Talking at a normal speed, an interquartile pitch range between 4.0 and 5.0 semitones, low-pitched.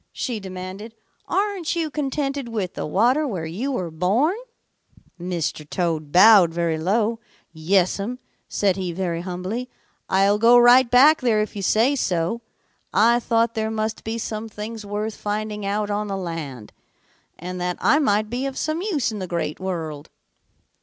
No: average, 160 wpm; average, 4.7 semitones; high, 210 Hz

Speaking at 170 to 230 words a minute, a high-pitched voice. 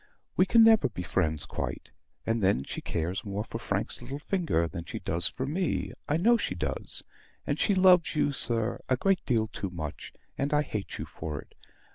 No: average, 200 wpm; low, 115 Hz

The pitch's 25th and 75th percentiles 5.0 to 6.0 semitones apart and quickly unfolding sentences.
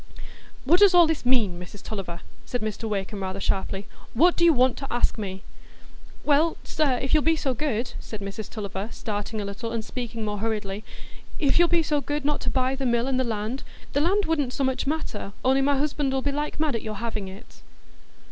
Yes: wide, 5.6 semitones; fast, 210 wpm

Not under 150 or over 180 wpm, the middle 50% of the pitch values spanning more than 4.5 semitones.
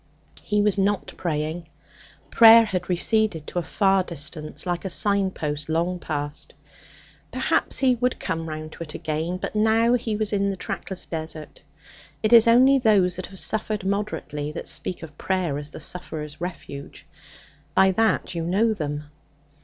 Yes: average, 160 wpm; average, 5.0 semitones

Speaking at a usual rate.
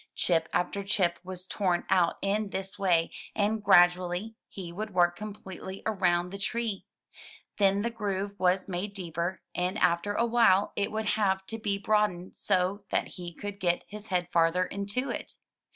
Yes: average, 165 wpm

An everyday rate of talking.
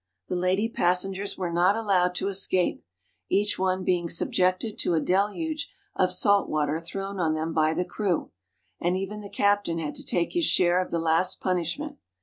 Yes: average, 180 wpm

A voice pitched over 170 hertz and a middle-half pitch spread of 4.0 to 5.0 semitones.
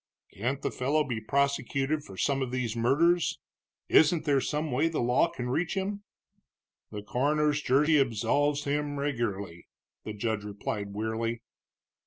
No: low, 135 Hz; average, 4.6 semitones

